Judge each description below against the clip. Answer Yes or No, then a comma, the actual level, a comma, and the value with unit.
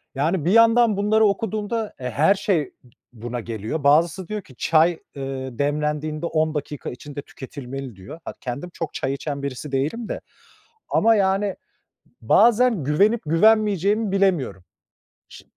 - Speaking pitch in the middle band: Yes, medium, 160 Hz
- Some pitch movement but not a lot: No, wide, 6.8 semitones